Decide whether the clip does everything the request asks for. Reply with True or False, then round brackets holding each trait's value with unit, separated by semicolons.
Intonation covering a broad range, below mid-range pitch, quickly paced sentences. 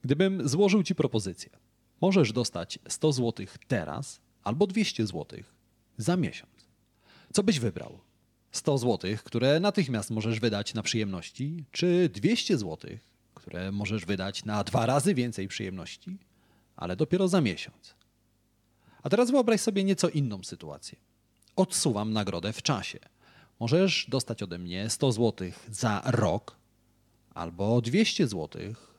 False (7.3 semitones; 120 Hz; 130 wpm)